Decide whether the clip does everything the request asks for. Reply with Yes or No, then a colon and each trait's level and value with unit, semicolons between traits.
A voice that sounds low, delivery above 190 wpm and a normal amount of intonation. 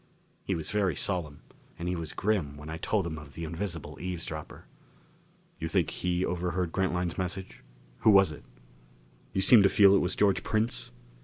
No: very low, 90 Hz; average, 175 wpm; average, 3.0 semitones